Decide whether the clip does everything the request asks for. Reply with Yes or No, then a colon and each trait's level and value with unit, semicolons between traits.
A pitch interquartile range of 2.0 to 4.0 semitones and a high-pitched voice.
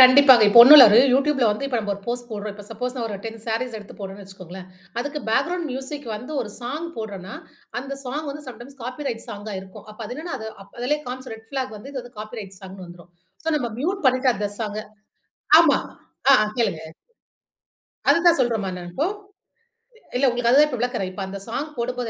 No: average, 4.5 semitones; high, 240 Hz